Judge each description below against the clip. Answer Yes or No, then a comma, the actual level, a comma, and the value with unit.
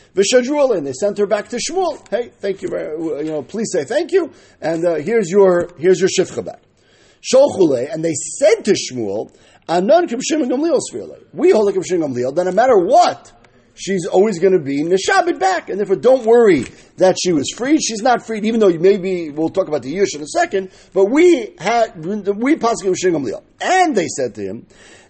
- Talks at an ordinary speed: Yes, average, 185 wpm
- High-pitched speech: Yes, high, 220 Hz